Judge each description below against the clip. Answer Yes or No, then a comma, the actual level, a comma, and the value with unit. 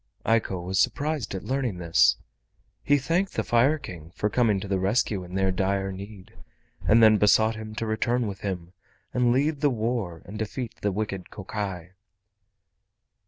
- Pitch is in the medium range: No, low, 105 Hz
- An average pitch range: Yes, average, 4.0 semitones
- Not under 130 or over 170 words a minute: Yes, average, 165 wpm